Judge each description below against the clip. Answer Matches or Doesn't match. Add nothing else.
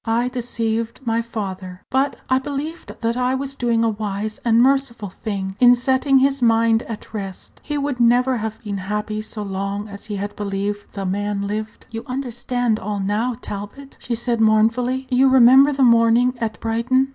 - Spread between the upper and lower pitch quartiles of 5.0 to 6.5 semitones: Doesn't match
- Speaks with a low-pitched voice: Doesn't match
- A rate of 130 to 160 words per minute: Doesn't match